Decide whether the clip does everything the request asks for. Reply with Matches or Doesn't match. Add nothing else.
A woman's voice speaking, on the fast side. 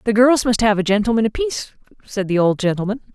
Matches